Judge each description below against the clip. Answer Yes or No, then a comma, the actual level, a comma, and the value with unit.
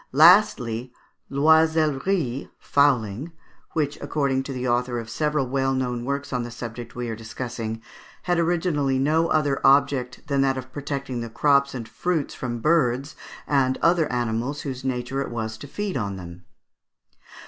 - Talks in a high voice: No, low, 135 Hz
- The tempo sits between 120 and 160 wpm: Yes, average, 155 wpm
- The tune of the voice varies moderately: Yes, average, 3.4 semitones